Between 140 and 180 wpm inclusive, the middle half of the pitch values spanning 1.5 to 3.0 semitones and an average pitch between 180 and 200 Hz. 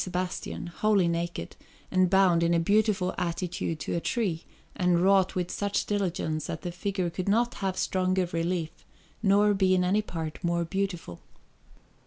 Yes: average, 160 wpm; narrow, 2.4 semitones; medium, 185 Hz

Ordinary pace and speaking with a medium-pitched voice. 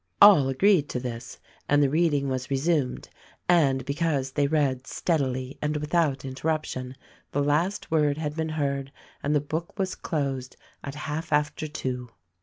Yes: average, 160 wpm; medium, 145 Hz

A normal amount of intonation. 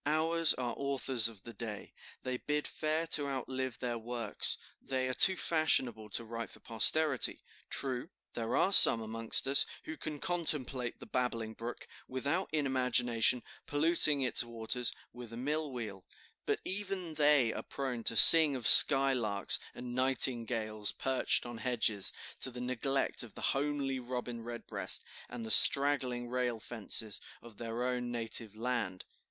Yes: average, 3.2 semitones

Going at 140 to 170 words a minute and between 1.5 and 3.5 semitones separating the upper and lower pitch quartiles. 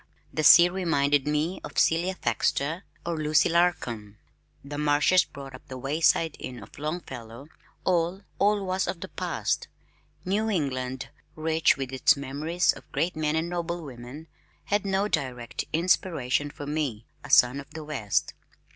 No: average, 155 wpm; average, 4.3 semitones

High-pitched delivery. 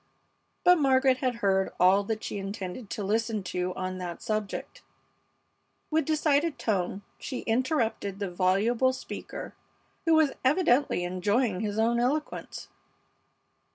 Yes: high, 220 Hz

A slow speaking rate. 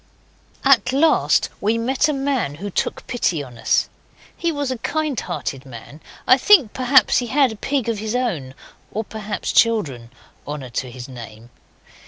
No: average, 170 wpm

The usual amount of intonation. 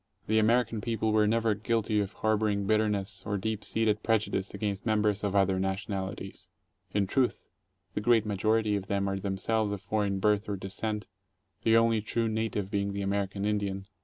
No: narrow, 1.8 semitones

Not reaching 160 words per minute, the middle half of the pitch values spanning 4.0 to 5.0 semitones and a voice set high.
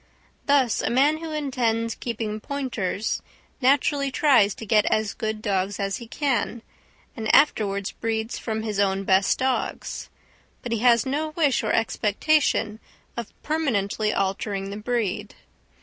Yes: average, 140 wpm; average, 4.4 semitones; high, 225 Hz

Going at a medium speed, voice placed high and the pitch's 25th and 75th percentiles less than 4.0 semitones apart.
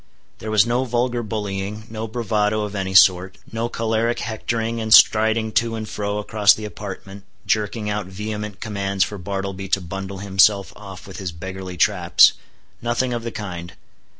No: average, 165 wpm; low, 105 Hz; narrow, 2.4 semitones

